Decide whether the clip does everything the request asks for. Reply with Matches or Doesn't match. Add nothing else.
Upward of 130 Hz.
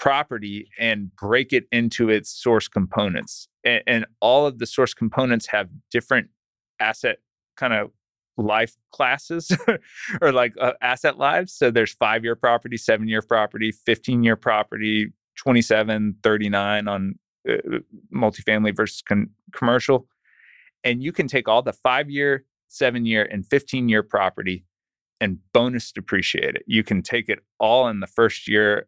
Doesn't match